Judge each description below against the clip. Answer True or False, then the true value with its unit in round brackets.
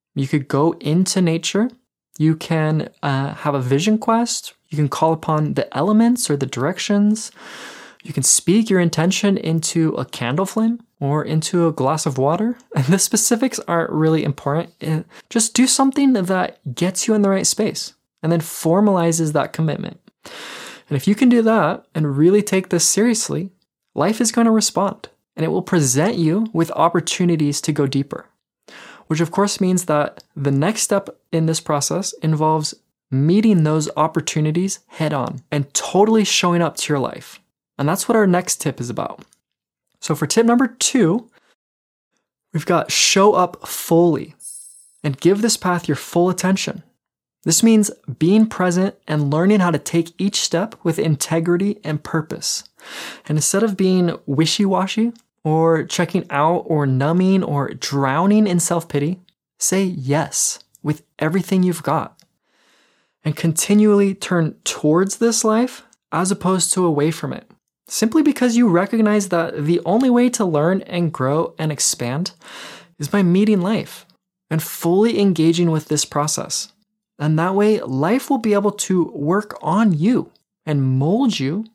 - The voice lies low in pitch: False (175 Hz)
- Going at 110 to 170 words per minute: True (160 wpm)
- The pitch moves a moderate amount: True (4.9 semitones)